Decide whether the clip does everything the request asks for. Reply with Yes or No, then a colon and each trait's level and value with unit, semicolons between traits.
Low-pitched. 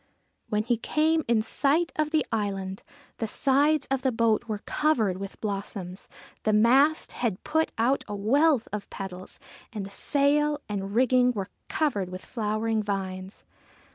No: high, 225 Hz